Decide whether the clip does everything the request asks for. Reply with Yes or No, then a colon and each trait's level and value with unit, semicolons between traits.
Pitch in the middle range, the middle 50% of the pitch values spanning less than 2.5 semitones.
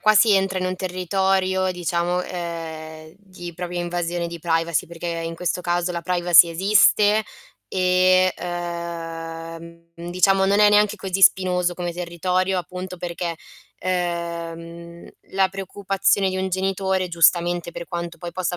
Yes: medium, 175 Hz; narrow, 1.7 semitones